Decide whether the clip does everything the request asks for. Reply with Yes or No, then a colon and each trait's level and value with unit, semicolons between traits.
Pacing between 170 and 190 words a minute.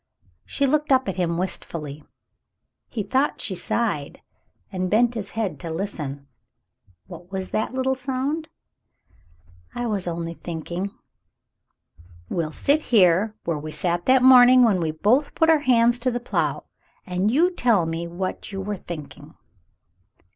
No: average, 150 wpm